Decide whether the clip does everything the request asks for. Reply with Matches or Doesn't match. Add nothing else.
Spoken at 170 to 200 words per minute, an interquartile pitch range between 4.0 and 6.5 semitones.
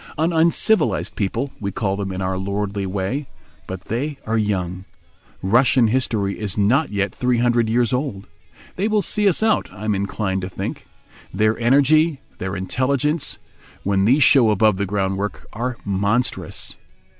Doesn't match